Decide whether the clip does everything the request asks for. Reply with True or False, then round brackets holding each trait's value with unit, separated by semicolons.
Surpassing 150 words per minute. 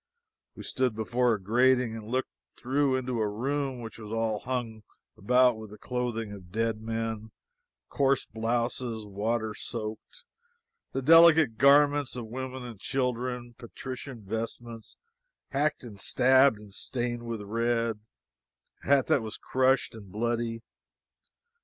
False (135 wpm)